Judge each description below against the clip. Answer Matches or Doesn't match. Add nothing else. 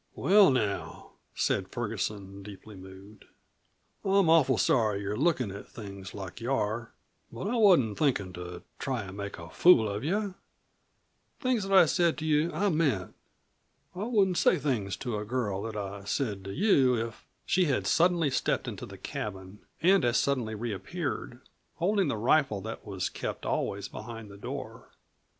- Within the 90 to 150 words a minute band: Doesn't match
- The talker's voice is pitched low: Matches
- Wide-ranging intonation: Matches